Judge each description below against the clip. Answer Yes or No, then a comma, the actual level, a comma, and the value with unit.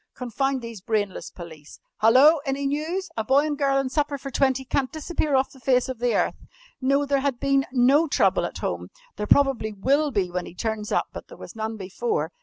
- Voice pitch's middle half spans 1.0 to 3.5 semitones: No, average, 4.2 semitones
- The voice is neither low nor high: No, very high, 265 Hz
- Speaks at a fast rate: Yes, fast, 210 wpm